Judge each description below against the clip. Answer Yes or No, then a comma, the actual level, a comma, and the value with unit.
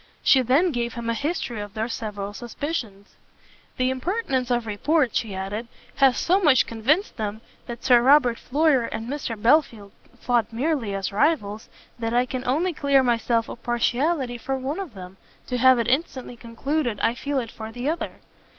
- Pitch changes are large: No, average, 3.8 semitones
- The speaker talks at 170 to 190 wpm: Yes, average, 180 wpm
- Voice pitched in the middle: No, high, 245 Hz